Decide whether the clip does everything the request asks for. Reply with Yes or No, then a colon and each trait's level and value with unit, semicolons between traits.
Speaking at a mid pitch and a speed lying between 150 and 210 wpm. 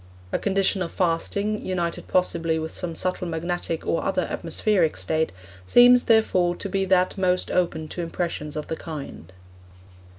Yes: medium, 175 Hz; average, 155 wpm